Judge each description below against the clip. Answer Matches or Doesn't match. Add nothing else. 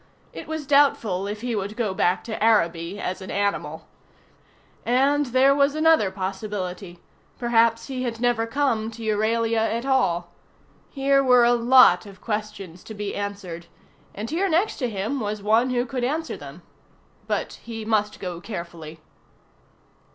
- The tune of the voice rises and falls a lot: Doesn't match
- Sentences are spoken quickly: Doesn't match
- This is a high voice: Matches